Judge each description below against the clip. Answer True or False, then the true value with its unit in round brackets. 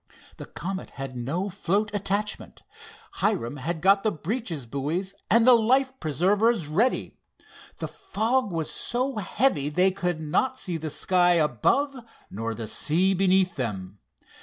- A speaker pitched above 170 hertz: True (185 Hz)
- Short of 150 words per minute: True (135 wpm)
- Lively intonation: True (6.0 semitones)